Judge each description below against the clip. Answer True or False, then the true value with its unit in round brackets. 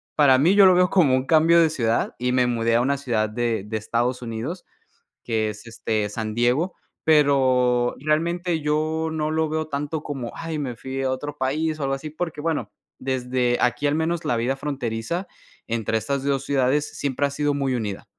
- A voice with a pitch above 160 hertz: False (135 Hz)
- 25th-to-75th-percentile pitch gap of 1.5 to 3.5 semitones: False (4.2 semitones)